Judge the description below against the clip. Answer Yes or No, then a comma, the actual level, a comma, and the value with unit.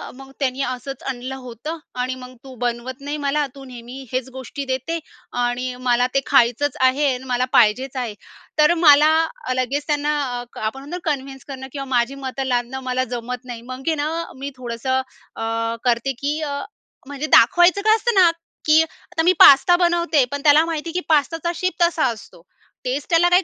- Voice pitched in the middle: No, very high, 270 Hz